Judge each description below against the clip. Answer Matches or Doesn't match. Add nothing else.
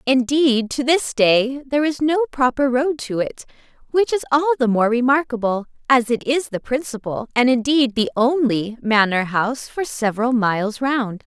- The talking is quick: Doesn't match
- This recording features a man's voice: Doesn't match